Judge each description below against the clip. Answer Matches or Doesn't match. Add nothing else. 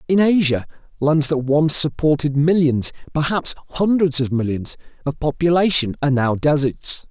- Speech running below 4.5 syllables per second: Doesn't match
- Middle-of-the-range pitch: Matches